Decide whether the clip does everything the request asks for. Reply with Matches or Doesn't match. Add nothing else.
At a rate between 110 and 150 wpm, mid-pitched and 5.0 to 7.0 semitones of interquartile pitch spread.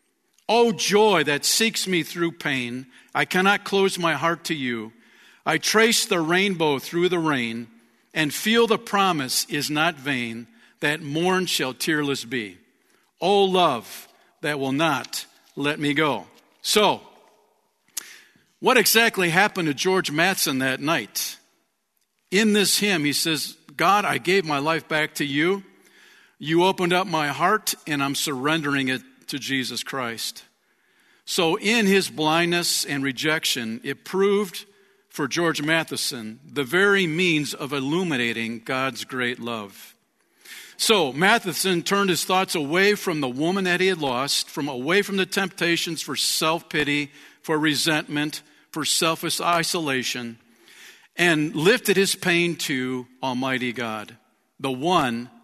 Matches